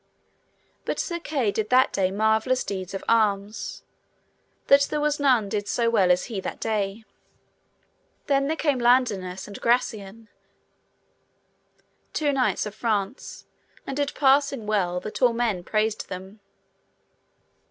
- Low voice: No, high, 220 Hz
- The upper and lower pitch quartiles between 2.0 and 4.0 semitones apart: No, average, 4.6 semitones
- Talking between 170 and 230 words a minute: No, slow, 135 wpm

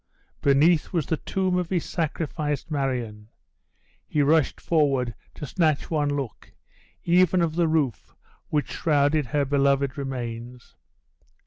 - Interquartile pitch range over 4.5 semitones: No, average, 3.2 semitones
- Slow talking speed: Yes, slow, 125 wpm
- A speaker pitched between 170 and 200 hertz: No, medium, 145 Hz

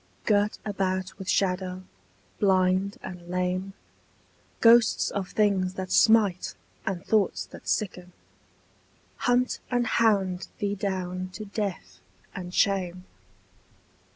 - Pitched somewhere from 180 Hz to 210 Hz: Yes, high, 190 Hz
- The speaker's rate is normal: No, slow, 105 wpm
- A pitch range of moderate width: No, narrow, 2.1 semitones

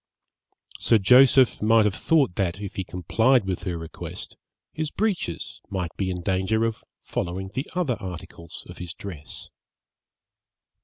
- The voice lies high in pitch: No, low, 100 Hz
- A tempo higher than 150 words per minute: No, average, 145 wpm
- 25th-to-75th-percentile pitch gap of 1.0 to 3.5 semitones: No, wide, 5.6 semitones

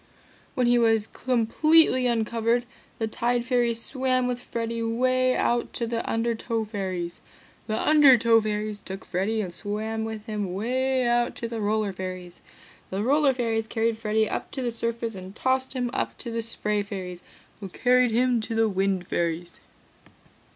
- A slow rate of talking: No, average, 165 wpm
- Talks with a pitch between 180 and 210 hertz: No, high, 225 Hz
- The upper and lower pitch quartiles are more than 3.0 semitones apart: No, average, 2.7 semitones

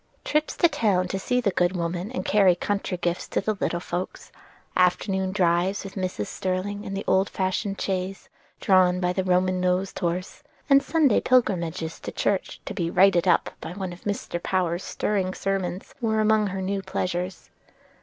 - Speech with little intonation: Yes, narrow, 1.8 semitones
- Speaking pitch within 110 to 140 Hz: No, medium, 185 Hz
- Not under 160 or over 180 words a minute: Yes, average, 175 wpm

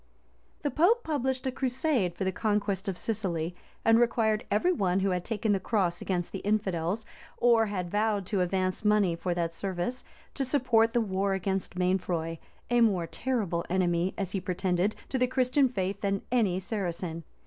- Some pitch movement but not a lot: Yes, average, 4.1 semitones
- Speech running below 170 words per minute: No, average, 175 wpm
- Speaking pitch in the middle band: No, high, 195 Hz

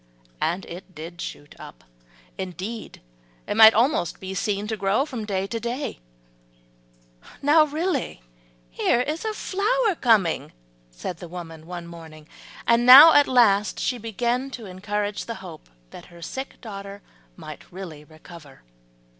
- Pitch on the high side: Yes, high, 205 Hz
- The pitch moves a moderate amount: No, wide, 6.1 semitones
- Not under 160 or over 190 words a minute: No, average, 145 wpm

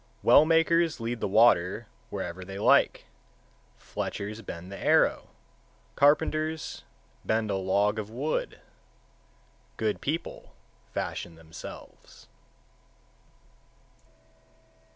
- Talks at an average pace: No, slow, 90 wpm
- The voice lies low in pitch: Yes, low, 110 Hz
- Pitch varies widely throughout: Yes, wide, 7.2 semitones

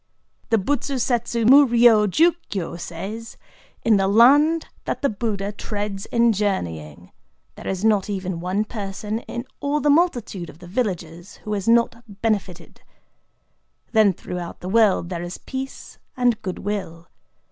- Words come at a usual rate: Yes, average, 145 wpm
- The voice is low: No, high, 210 Hz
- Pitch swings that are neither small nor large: Yes, average, 4.1 semitones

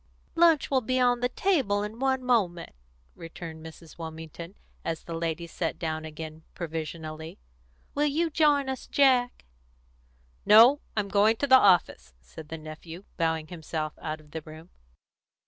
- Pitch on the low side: No, medium, 170 Hz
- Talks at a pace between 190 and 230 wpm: No, average, 150 wpm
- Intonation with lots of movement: Yes, wide, 7.8 semitones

